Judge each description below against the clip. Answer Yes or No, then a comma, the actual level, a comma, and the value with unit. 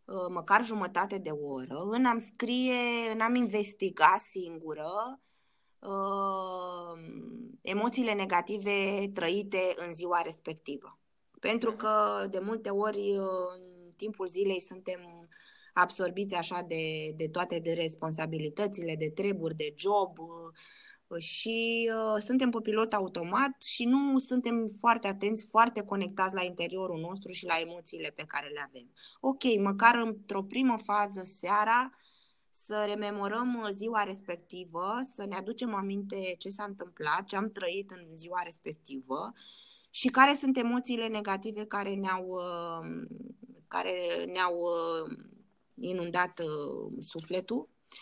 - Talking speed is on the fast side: No, average, 125 wpm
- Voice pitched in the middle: No, high, 195 Hz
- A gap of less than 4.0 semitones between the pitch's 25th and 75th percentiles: No, average, 4.3 semitones